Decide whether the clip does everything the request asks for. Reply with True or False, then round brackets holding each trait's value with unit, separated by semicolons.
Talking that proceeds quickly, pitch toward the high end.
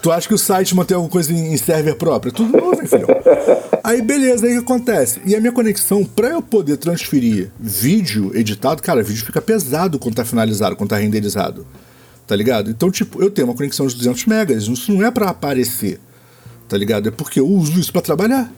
False (215 wpm; 175 Hz)